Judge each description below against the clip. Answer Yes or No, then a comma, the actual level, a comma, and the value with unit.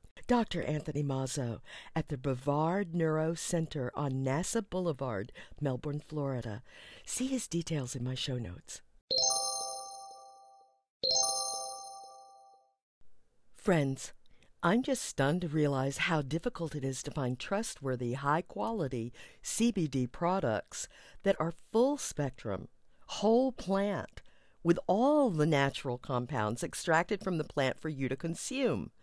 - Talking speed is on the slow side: Yes, slow, 115 wpm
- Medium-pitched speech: Yes, medium, 145 Hz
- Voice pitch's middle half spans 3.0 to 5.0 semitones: Yes, average, 4.7 semitones